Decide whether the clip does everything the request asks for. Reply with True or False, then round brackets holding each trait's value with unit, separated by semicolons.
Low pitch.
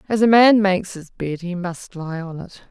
False (185 Hz)